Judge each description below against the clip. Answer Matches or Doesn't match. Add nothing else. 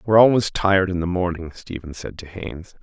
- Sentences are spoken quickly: Matches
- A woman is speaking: Doesn't match